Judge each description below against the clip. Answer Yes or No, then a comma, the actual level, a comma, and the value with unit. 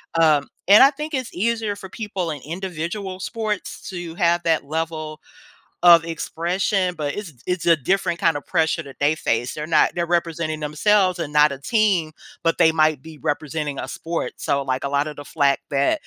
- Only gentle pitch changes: No, average, 3.6 semitones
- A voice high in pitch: No, medium, 165 Hz